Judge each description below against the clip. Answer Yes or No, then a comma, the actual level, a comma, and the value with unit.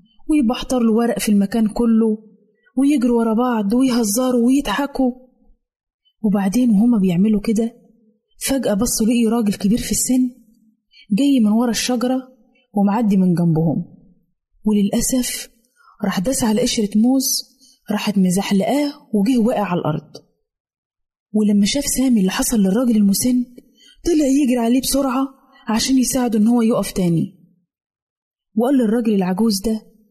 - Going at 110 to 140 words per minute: Yes, average, 120 wpm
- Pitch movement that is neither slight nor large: Yes, average, 3.2 semitones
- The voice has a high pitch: Yes, high, 230 Hz